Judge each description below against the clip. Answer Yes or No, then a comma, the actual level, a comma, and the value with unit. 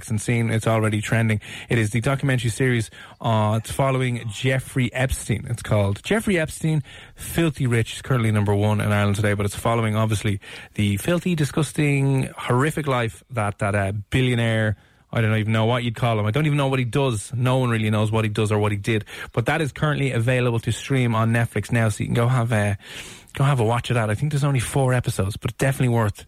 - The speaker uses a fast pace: Yes, fast, 225 wpm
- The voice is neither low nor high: No, low, 115 Hz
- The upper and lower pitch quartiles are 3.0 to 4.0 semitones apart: Yes, average, 3.5 semitones